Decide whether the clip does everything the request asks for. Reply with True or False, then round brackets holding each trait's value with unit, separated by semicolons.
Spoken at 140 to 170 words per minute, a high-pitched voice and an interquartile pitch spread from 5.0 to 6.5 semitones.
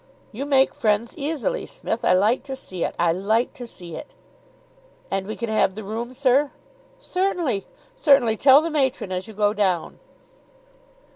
True (165 wpm; 235 Hz; 5.4 semitones)